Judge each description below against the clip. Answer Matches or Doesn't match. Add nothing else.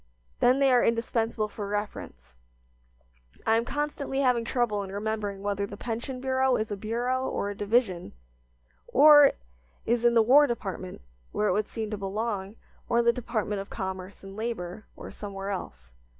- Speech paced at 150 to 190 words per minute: Matches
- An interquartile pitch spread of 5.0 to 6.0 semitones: Doesn't match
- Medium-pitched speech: Doesn't match